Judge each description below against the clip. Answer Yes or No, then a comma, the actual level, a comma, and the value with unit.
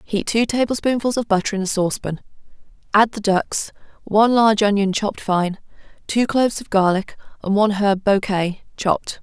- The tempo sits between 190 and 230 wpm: No, average, 165 wpm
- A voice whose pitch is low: No, high, 205 Hz